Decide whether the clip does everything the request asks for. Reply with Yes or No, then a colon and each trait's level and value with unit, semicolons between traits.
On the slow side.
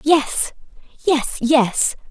Yes: slow, 85 wpm